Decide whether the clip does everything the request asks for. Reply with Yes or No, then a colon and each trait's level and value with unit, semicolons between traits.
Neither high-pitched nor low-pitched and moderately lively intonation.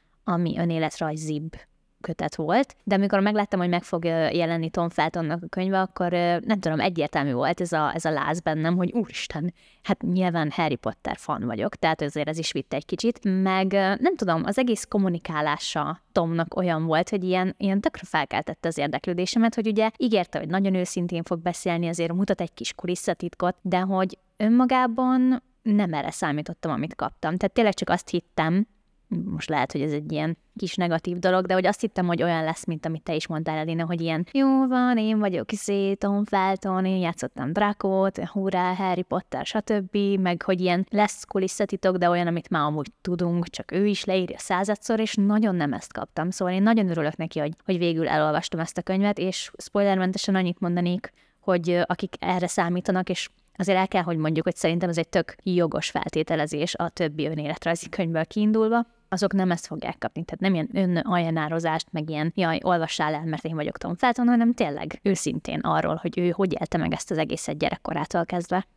Yes: medium, 180 Hz; average, 3.3 semitones